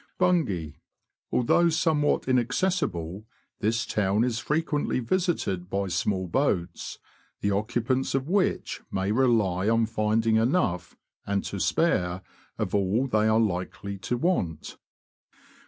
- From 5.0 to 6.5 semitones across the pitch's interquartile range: Yes, wide, 5.6 semitones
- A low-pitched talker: Yes, low, 110 Hz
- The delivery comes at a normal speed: No, slow, 120 wpm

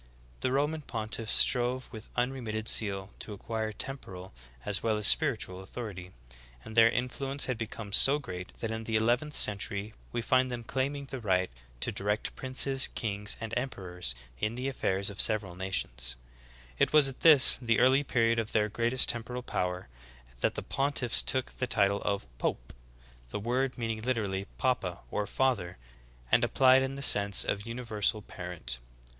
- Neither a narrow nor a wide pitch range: Yes, average, 4.2 semitones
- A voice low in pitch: Yes, low, 115 Hz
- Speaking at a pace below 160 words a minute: No, average, 170 wpm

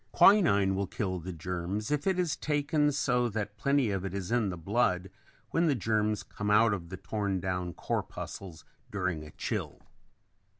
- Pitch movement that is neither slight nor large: Yes, average, 4.9 semitones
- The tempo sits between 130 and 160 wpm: No, average, 175 wpm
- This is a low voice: Yes, low, 105 Hz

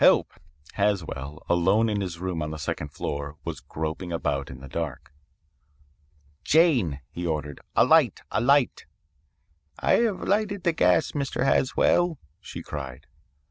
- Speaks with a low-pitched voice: Yes, very low, 85 Hz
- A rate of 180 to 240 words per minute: No, average, 140 wpm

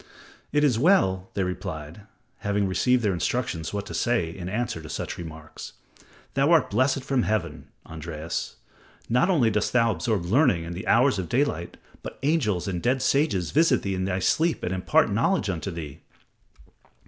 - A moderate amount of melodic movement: No, wide, 6.6 semitones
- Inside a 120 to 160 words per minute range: No, average, 170 wpm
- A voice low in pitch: Yes, low, 100 Hz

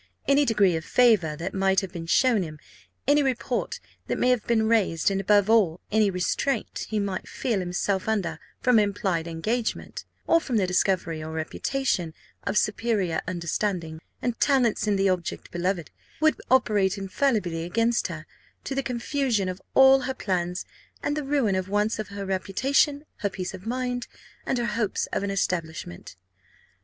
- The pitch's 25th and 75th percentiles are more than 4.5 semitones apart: Yes, average, 4.9 semitones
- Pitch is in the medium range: No, high, 200 Hz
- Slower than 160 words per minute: No, average, 170 wpm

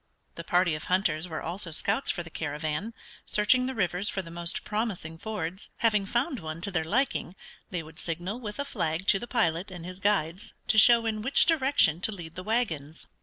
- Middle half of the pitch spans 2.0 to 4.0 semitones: No, average, 5.0 semitones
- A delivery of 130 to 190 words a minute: No, fast, 205 wpm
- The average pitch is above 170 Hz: Yes, medium, 185 Hz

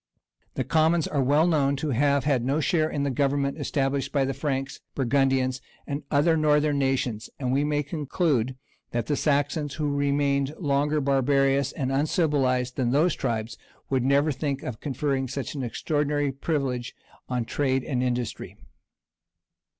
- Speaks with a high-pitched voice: No, medium, 140 Hz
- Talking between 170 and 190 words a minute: No, average, 155 wpm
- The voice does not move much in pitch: Yes, narrow, 1.9 semitones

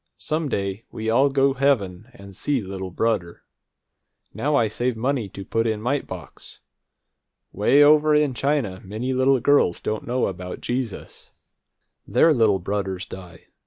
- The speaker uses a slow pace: No, average, 150 wpm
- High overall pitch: No, low, 115 Hz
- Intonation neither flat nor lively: No, wide, 5.9 semitones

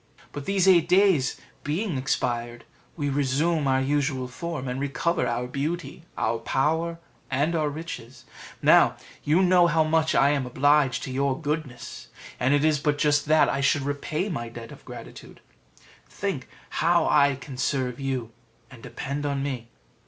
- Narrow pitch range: No, average, 3.2 semitones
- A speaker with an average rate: Yes, average, 160 wpm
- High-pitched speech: No, medium, 145 Hz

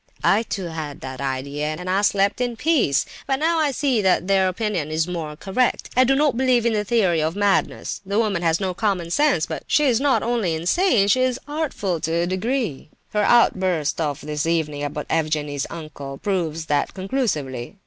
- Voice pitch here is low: No, medium, 185 Hz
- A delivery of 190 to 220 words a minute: Yes, average, 200 wpm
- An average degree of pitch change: No, wide, 7.0 semitones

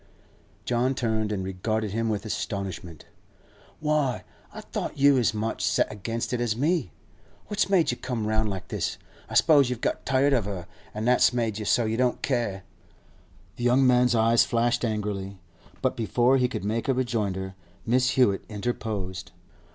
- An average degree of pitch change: Yes, average, 3.1 semitones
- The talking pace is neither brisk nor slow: Yes, average, 175 wpm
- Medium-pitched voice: No, low, 115 Hz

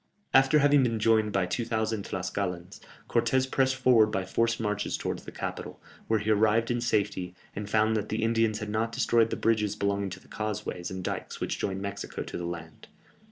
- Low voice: Yes, low, 110 Hz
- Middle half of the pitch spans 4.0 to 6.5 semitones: No, narrow, 2.4 semitones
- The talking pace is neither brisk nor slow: Yes, average, 195 wpm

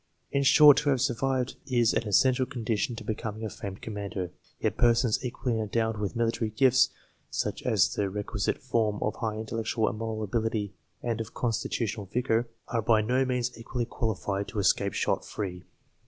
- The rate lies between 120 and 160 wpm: No, average, 170 wpm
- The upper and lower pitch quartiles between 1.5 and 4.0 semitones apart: Yes, narrow, 2.6 semitones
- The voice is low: Yes, low, 115 Hz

